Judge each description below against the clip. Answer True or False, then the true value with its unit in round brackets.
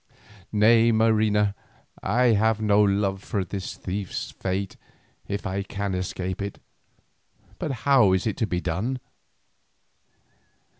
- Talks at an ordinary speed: False (120 wpm)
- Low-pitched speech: True (100 Hz)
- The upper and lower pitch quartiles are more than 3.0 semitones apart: False (2.5 semitones)